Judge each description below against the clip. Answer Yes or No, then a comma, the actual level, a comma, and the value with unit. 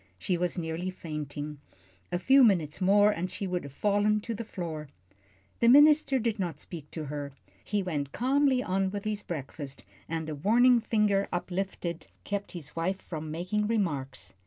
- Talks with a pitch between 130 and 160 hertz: No, medium, 185 Hz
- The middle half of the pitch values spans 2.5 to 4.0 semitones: No, average, 5.1 semitones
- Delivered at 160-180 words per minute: Yes, average, 170 wpm